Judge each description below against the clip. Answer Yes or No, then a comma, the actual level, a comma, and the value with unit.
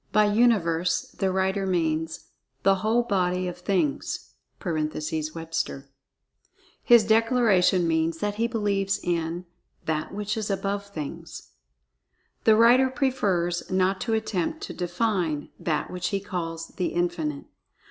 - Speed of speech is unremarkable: No, slow, 125 wpm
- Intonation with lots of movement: No, average, 4.0 semitones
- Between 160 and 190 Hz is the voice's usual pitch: Yes, medium, 185 Hz